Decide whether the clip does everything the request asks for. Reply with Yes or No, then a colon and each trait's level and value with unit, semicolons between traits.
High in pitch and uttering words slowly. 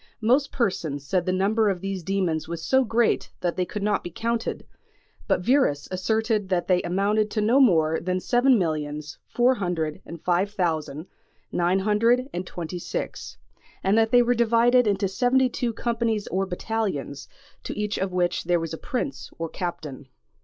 No: high, 195 Hz; average, 175 wpm